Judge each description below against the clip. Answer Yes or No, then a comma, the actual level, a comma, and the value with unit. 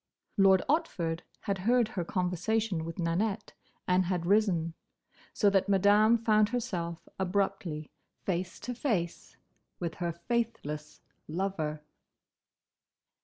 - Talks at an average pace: No, slow, 110 wpm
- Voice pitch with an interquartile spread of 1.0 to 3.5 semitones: No, average, 4.0 semitones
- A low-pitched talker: No, high, 190 Hz